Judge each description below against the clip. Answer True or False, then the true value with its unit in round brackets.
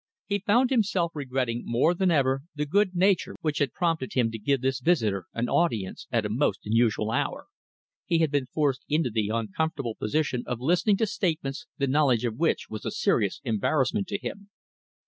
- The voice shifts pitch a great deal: True (6.6 semitones)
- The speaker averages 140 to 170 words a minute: False (185 wpm)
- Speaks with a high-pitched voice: False (140 Hz)